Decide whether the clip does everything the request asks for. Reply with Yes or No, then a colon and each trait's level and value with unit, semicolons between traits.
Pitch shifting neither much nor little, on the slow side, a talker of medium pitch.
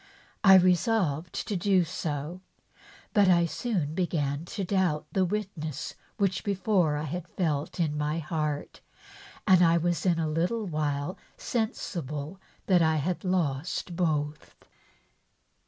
Yes: average, 3.6 semitones; slow, 130 wpm; medium, 170 Hz